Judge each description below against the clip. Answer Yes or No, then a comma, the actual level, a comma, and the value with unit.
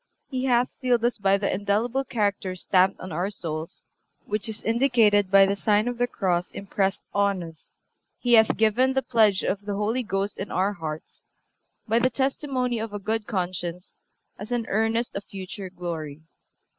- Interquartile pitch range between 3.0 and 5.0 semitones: Yes, average, 3.7 semitones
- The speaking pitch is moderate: No, high, 205 Hz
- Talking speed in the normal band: Yes, average, 175 wpm